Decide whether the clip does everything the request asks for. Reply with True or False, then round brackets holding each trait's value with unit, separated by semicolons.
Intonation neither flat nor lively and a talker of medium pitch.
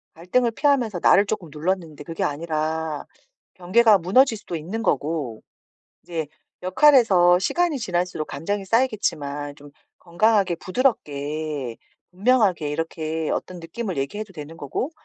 False (5.7 semitones; 175 Hz)